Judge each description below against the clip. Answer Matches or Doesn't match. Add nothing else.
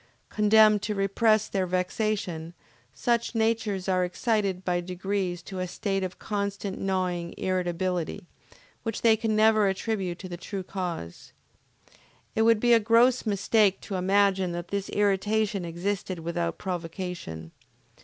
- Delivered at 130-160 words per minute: Matches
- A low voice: Doesn't match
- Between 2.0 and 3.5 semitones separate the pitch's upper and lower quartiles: Matches